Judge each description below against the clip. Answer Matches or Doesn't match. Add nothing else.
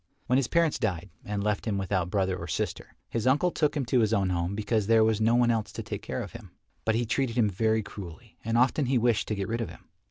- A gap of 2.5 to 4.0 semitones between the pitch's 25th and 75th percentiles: Matches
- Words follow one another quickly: Matches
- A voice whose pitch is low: Matches